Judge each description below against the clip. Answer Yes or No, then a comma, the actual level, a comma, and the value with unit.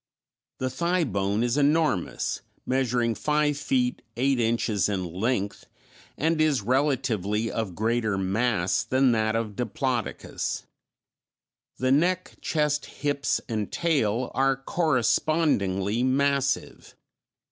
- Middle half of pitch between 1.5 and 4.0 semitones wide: No, average, 4.7 semitones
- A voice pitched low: Yes, low, 125 Hz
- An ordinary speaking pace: No, slow, 105 wpm